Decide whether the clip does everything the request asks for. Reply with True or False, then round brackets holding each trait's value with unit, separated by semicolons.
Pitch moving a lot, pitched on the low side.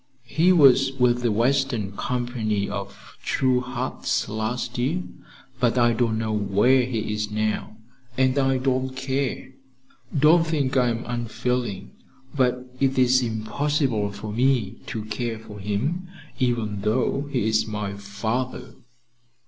False (3.4 semitones; 120 Hz)